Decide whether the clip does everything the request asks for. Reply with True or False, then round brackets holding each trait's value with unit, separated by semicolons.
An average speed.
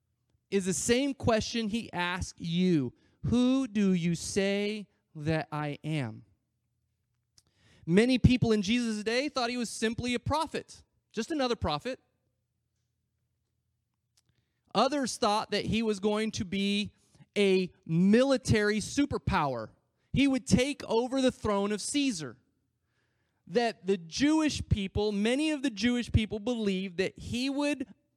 False (130 wpm)